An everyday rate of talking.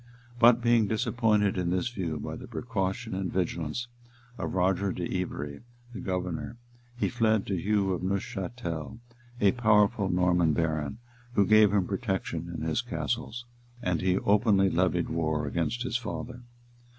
Yes: average, 150 wpm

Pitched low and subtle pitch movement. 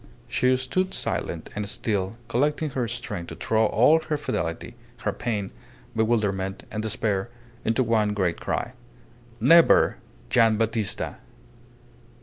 No: low, 110 Hz; average, 3.6 semitones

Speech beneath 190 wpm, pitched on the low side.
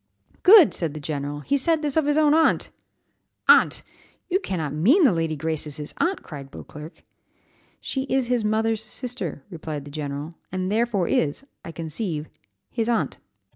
No: average, 175 wpm; medium, 185 Hz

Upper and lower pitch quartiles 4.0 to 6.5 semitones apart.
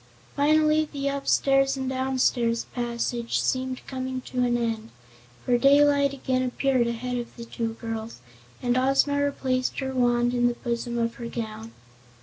No: narrow, 2.4 semitones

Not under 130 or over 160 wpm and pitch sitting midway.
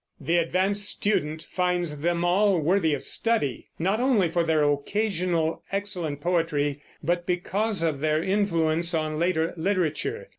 Yes: average, 140 wpm; medium, 175 Hz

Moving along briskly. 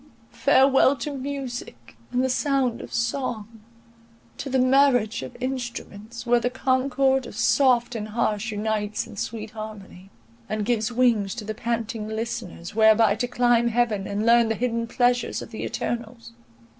No: average, 155 wpm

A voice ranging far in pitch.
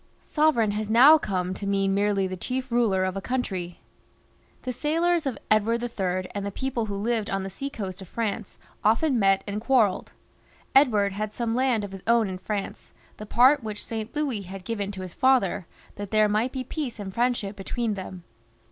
No: average, 4.0 semitones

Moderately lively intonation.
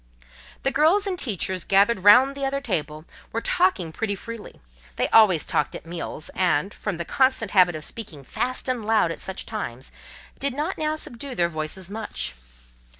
No: wide, 7.2 semitones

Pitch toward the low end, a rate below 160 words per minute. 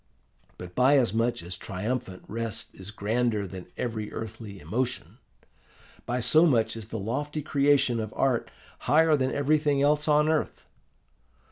Yes: low, 120 Hz; average, 145 wpm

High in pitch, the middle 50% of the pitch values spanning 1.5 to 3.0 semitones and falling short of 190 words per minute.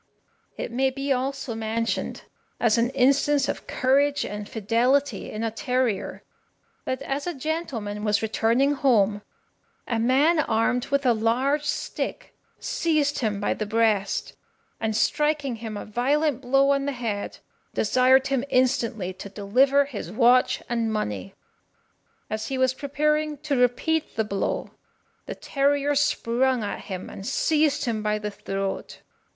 No: very high, 250 Hz; average, 4.2 semitones; average, 145 wpm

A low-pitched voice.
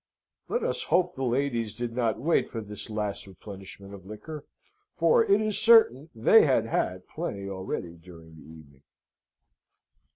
Yes: low, 110 Hz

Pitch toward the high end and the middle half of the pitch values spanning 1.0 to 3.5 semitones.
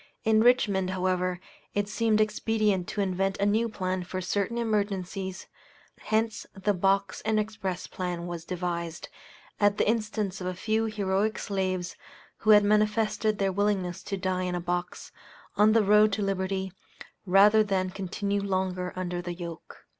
Yes: high, 195 Hz; narrow, 2.5 semitones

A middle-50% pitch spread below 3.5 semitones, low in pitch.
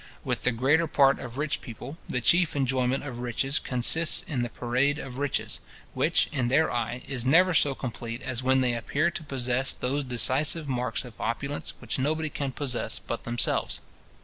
Yes: average, 2.8 semitones; low, 130 Hz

